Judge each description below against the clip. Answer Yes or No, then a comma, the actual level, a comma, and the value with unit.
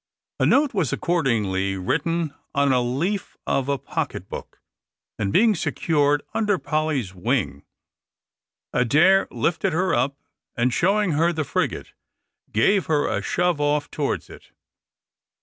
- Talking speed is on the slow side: Yes, slow, 130 wpm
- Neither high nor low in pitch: Yes, medium, 150 Hz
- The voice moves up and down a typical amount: No, wide, 5.9 semitones